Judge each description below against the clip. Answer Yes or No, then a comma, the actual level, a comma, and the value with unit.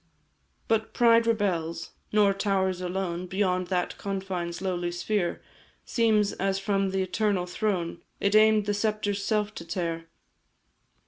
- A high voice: Yes, high, 195 Hz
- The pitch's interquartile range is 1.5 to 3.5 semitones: Yes, average, 2.8 semitones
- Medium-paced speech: No, slow, 130 wpm